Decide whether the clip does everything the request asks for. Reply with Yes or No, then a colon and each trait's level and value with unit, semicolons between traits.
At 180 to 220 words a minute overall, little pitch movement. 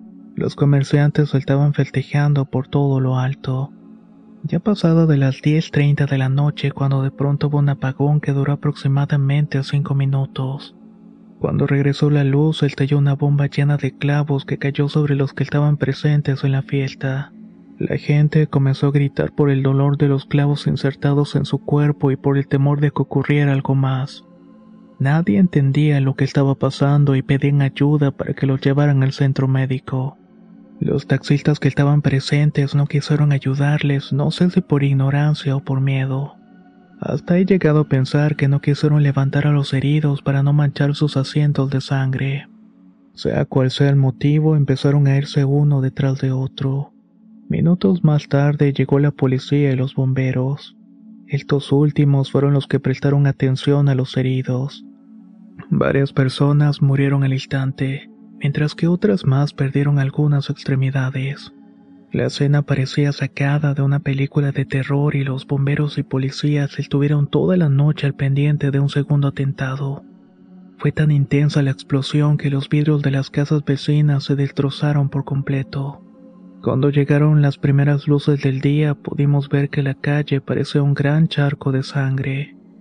No: average, 160 wpm; narrow, 1.3 semitones